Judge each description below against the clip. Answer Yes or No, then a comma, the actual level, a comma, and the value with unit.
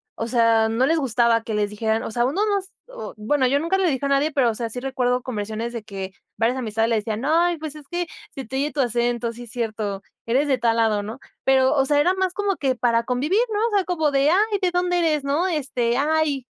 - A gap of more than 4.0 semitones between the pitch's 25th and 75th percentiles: Yes, average, 5.2 semitones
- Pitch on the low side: No, very high, 260 Hz